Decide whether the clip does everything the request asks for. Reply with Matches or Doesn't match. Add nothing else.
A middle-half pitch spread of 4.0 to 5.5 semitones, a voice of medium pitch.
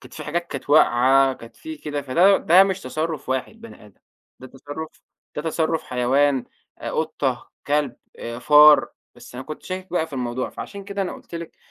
Matches